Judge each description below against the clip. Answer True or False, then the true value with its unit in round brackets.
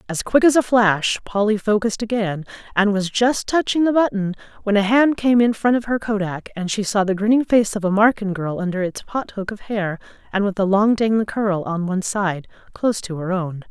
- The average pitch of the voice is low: False (205 Hz)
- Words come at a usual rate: False (230 wpm)